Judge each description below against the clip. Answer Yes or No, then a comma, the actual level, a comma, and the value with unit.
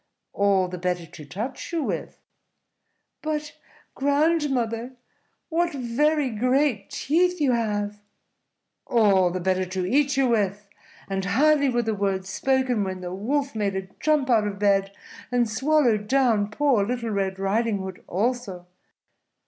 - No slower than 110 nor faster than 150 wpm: Yes, average, 140 wpm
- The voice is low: No, high, 225 Hz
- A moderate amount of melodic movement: No, wide, 5.8 semitones